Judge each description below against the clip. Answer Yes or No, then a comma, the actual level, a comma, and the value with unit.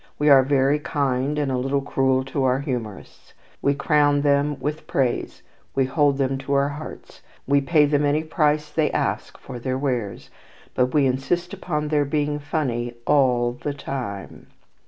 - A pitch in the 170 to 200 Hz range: No, medium, 140 Hz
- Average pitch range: No, narrow, 2.1 semitones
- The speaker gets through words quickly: No, average, 170 wpm